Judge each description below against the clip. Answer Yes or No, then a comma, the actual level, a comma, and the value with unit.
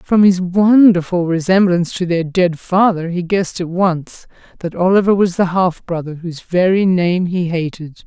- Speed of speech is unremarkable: Yes, average, 170 wpm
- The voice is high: No, medium, 180 Hz